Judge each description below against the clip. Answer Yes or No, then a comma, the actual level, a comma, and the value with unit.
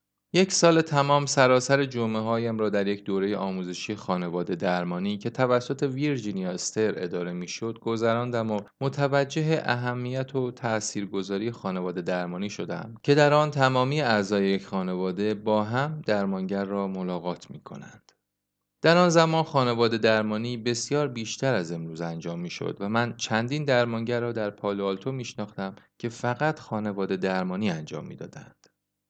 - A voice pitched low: Yes, low, 110 Hz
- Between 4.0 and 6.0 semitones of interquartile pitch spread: Yes, average, 4.8 semitones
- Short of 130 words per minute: No, average, 140 wpm